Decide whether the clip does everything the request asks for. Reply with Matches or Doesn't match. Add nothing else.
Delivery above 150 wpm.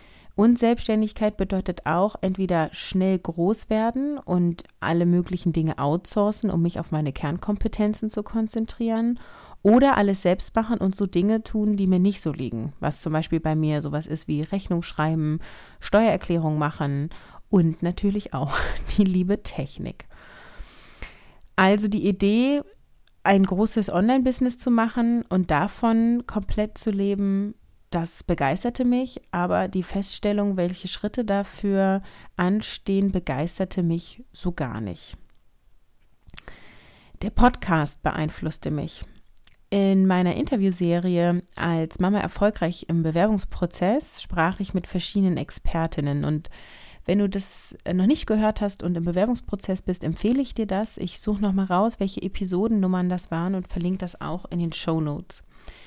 Doesn't match